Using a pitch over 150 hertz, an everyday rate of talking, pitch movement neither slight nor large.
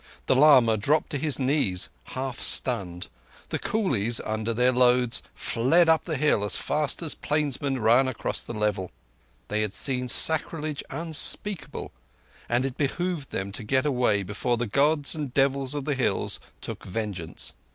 No: low, 130 Hz; average, 160 wpm; average, 4.7 semitones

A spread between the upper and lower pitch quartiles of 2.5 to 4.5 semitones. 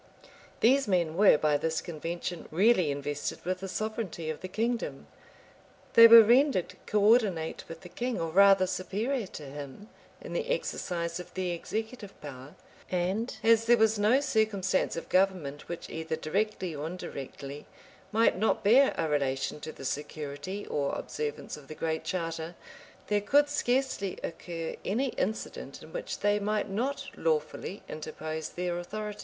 No: wide, 5.5 semitones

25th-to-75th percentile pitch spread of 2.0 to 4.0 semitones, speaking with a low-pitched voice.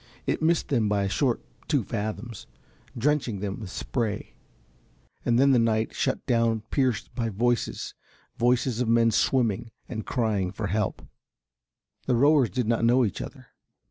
Yes: narrow, 2.6 semitones; low, 115 Hz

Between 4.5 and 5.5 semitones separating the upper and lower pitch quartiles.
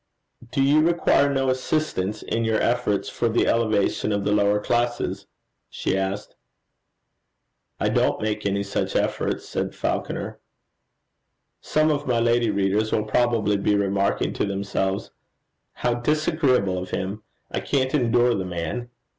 No: average, 3.7 semitones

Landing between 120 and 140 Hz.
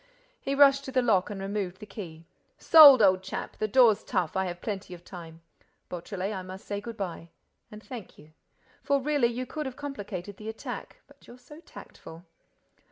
No: high, 205 Hz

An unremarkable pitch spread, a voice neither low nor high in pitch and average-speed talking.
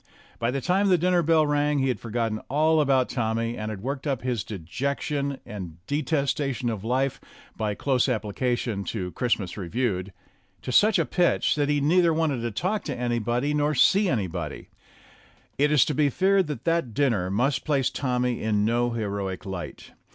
No: average, 5.0 semitones; low, 125 Hz; average, 180 wpm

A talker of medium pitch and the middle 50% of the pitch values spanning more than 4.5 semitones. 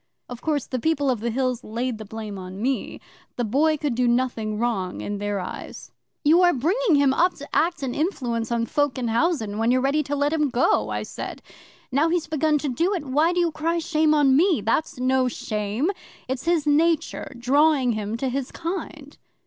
No: very high, 270 Hz; average, 4.9 semitones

